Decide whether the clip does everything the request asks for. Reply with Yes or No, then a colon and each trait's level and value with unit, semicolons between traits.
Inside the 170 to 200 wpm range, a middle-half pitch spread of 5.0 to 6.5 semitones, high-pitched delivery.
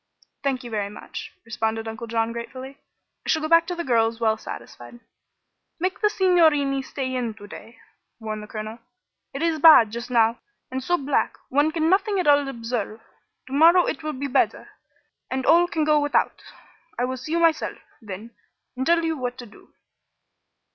Yes: average, 185 wpm; wide, 5.6 semitones; very high, 260 Hz